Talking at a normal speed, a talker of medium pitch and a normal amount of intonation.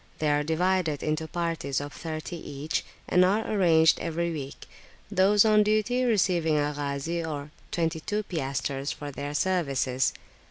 Yes: average, 150 wpm; medium, 160 Hz; average, 4.0 semitones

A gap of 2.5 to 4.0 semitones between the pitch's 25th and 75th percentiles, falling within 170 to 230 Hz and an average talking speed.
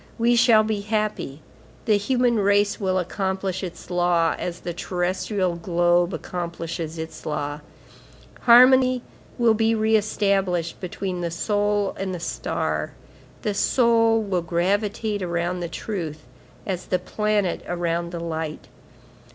No: average, 3.7 semitones; high, 190 Hz; slow, 130 wpm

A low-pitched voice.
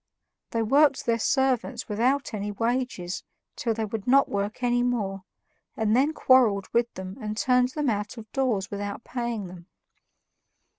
No: high, 230 Hz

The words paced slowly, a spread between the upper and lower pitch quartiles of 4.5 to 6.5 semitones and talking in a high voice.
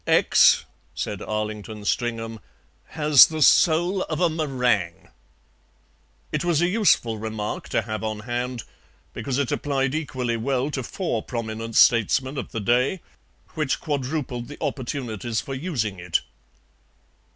No: slow, 130 wpm; average, 4.9 semitones; low, 125 Hz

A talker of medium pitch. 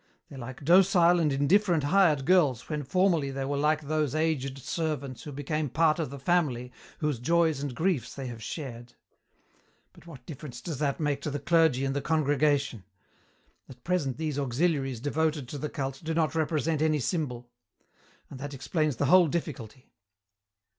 Yes: medium, 145 Hz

